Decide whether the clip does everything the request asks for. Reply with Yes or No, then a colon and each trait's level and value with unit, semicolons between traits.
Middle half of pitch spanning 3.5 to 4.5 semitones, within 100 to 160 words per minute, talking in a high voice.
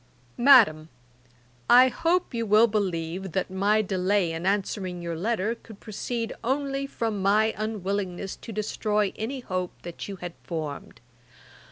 Yes: average, 3.8 semitones; average, 140 wpm; high, 205 Hz